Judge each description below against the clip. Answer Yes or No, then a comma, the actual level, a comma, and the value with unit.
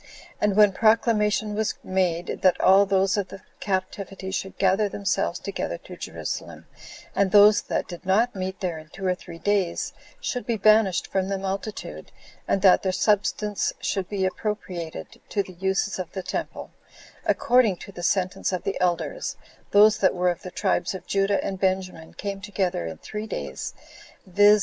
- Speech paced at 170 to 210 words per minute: Yes, average, 175 wpm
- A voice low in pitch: No, high, 195 Hz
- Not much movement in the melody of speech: Yes, narrow, 1.9 semitones